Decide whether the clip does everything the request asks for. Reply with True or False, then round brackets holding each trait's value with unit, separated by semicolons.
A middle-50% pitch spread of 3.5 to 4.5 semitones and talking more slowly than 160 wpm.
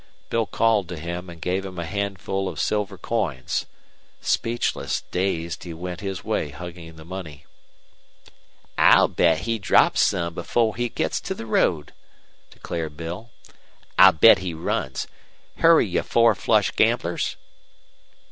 True (4.0 semitones; 140 wpm)